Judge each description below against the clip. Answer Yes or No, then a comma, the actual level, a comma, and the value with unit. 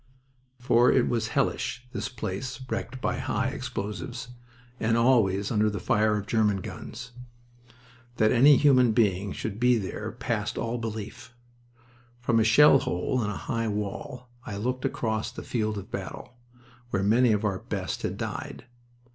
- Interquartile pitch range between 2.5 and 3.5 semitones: Yes, average, 2.8 semitones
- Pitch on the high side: No, low, 115 Hz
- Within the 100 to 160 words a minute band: Yes, average, 155 wpm